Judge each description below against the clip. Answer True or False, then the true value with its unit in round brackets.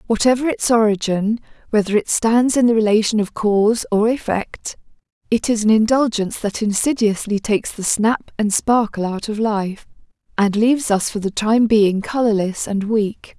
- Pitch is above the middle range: True (215 Hz)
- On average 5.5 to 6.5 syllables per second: False (4.8 syllables/s)